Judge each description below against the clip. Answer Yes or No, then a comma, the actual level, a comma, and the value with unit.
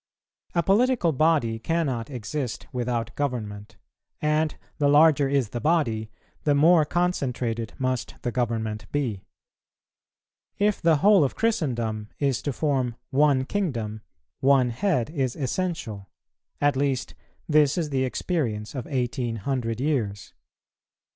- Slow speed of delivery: Yes, slow, 125 wpm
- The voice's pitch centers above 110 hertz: Yes, low, 135 Hz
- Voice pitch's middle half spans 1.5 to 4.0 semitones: No, average, 4.7 semitones